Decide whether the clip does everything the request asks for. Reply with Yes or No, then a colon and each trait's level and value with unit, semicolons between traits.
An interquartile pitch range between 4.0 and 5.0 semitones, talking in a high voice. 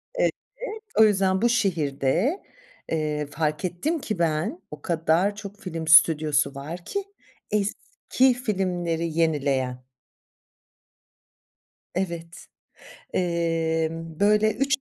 No: average, 4.6 semitones; medium, 170 Hz